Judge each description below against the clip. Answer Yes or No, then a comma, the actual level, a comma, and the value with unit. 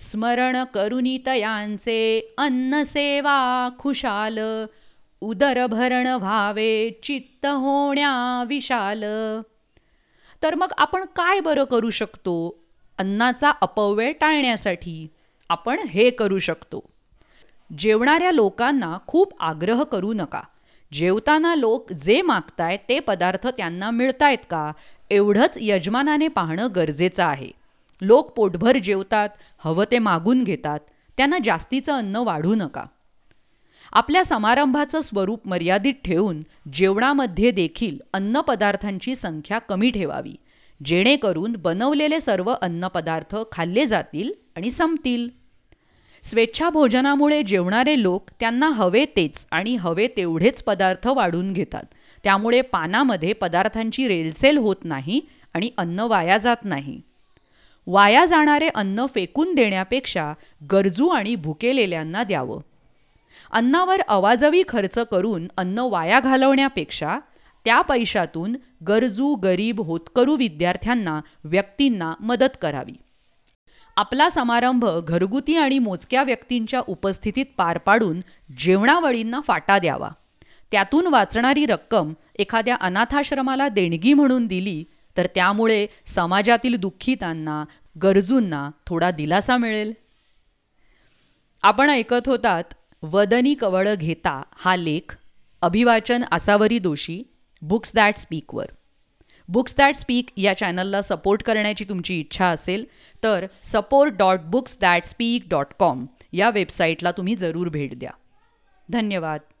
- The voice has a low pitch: No, high, 220 Hz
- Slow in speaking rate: Yes, slow, 105 wpm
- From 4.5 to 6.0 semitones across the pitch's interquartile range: Yes, wide, 5.6 semitones